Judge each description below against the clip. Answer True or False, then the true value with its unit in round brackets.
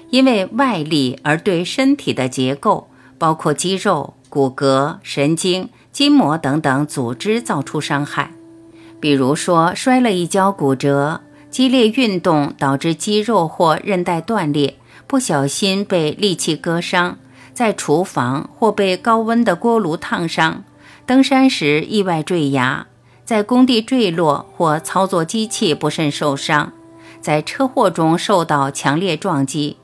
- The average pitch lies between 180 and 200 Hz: False (165 Hz)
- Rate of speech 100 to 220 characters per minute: True (205 characters per minute)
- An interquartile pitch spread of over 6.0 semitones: True (6.5 semitones)